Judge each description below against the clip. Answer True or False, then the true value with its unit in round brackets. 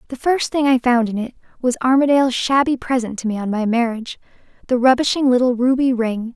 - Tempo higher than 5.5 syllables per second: True (6.0 syllables/s)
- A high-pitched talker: True (250 Hz)